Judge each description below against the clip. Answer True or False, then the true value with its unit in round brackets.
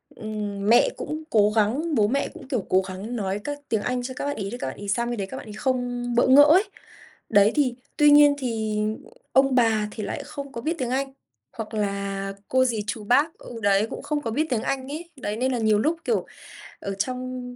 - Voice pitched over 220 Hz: True (240 Hz)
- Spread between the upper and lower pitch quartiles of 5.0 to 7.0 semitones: False (4.4 semitones)